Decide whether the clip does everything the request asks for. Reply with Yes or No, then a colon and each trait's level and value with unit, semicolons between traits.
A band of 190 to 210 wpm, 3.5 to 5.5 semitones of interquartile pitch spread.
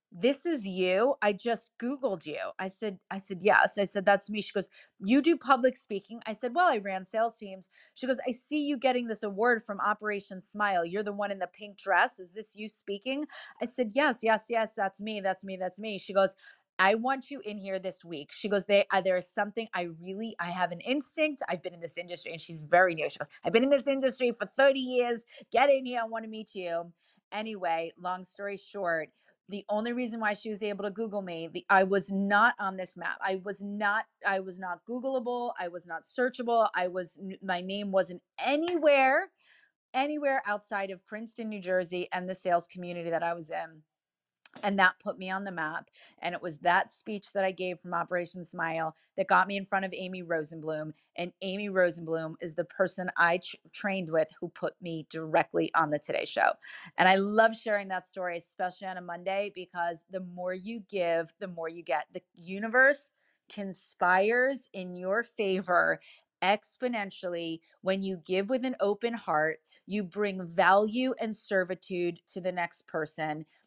Yes: fast, 205 wpm; average, 3.9 semitones